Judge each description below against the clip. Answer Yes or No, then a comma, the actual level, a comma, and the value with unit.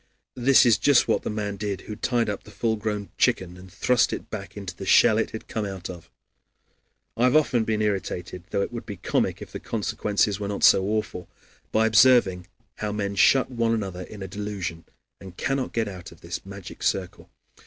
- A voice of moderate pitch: No, low, 105 Hz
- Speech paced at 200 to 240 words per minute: Yes, fast, 205 wpm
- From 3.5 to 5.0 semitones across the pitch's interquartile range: No, average, 2.8 semitones